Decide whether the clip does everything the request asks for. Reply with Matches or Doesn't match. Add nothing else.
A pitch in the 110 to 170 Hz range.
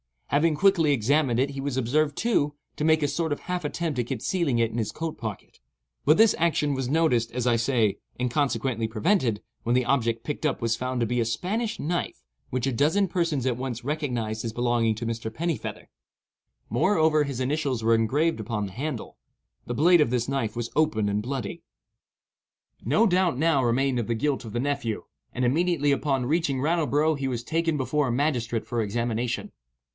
Matches